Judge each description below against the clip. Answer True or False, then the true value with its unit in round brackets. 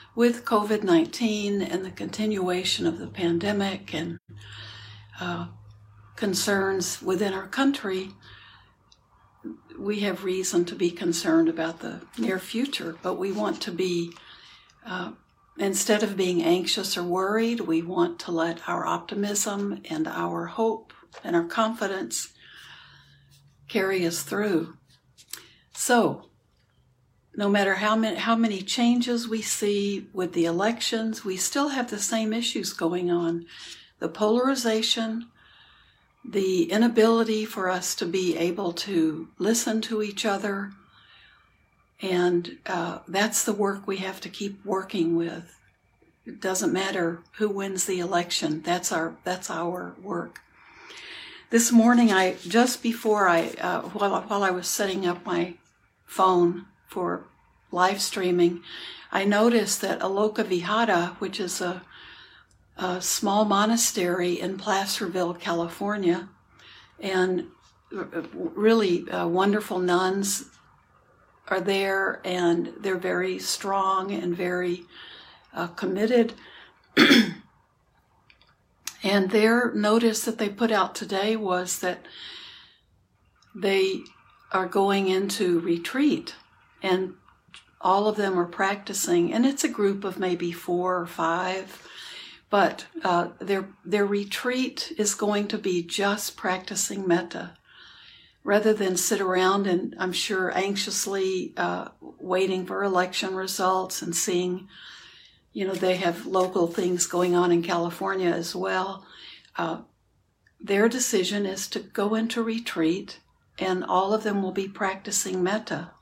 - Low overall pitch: False (190 Hz)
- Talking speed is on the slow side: True (125 wpm)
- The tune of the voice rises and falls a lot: False (2.9 semitones)